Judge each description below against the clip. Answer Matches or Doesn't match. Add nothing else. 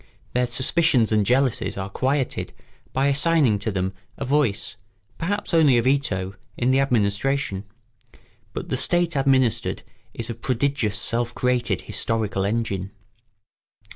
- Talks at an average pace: Doesn't match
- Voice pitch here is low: Matches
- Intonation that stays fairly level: Doesn't match